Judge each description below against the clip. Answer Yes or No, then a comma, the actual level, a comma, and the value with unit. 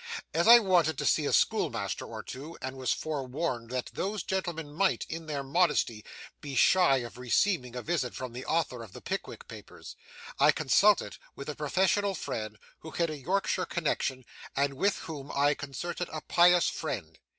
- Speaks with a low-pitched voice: No, medium, 150 Hz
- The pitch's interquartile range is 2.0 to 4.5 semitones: No, average, 4.9 semitones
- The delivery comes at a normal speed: Yes, average, 175 wpm